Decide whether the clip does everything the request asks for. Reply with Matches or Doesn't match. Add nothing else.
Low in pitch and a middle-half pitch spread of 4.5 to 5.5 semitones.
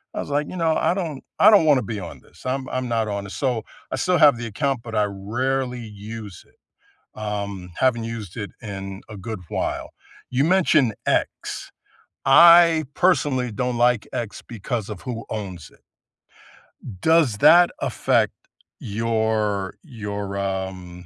Matches